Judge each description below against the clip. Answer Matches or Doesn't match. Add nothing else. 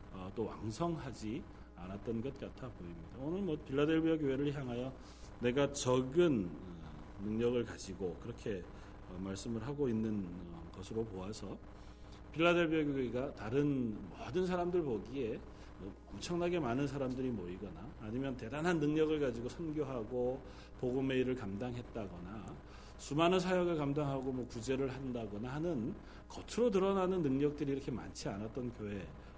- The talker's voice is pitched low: Matches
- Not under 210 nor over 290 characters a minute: Doesn't match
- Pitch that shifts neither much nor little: Doesn't match